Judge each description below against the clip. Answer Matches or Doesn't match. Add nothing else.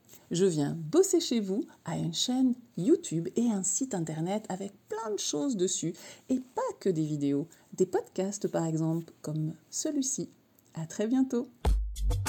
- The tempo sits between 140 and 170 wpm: Matches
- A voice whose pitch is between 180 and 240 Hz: Matches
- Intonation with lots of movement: Matches